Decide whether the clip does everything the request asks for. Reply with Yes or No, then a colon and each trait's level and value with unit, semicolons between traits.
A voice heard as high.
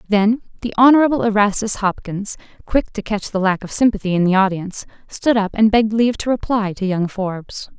Yes: high, 210 Hz